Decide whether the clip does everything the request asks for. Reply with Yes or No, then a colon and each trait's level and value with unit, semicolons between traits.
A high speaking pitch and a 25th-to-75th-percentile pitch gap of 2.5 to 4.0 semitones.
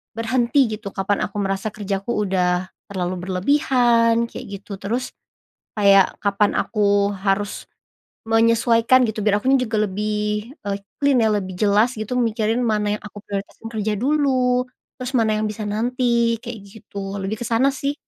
Yes: high, 215 Hz; average, 2.8 semitones